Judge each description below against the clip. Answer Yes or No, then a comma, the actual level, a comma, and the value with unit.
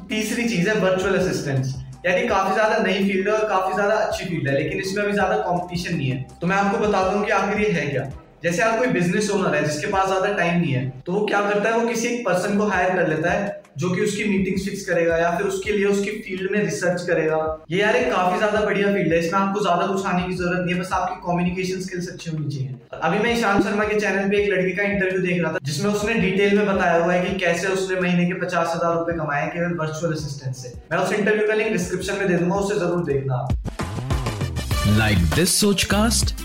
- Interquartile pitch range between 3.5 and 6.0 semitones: No, average, 3.0 semitones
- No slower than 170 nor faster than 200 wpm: Yes, average, 185 wpm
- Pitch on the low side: No, medium, 185 Hz